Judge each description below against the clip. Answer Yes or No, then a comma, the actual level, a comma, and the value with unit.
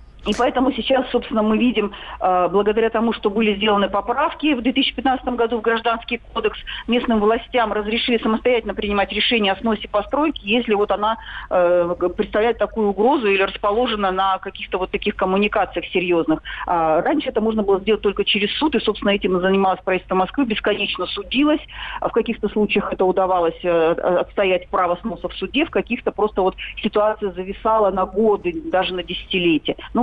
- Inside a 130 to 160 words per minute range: Yes, average, 155 wpm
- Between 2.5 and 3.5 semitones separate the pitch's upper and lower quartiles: Yes, average, 3.2 semitones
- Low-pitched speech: No, high, 210 Hz